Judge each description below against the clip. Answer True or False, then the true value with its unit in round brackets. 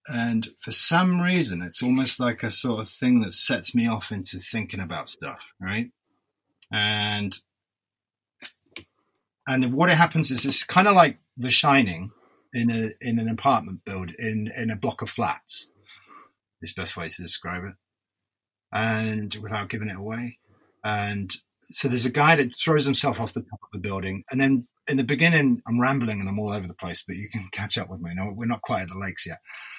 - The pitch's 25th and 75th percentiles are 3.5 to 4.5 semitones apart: True (4.2 semitones)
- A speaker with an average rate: True (195 wpm)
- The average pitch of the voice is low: True (110 Hz)